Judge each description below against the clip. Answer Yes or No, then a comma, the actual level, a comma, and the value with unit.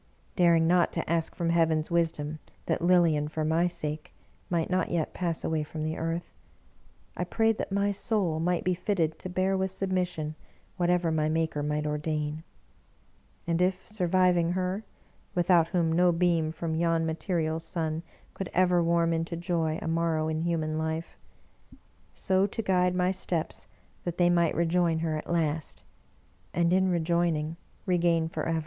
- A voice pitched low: No, medium, 170 Hz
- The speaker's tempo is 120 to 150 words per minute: No, average, 165 wpm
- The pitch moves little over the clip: Yes, narrow, 2.0 semitones